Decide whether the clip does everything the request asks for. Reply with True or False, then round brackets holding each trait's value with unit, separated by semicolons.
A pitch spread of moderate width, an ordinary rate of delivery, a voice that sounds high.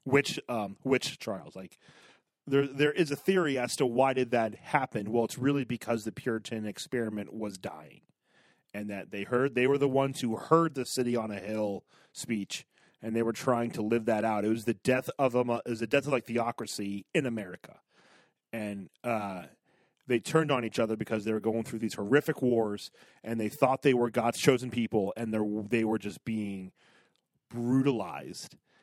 False (3.2 semitones; 195 wpm; 115 Hz)